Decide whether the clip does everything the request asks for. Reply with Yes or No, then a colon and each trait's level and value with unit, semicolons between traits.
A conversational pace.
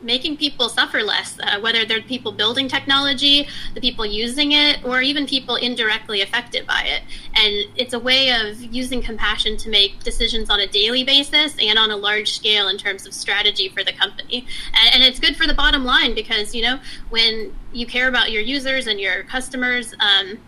Yes: average, 195 wpm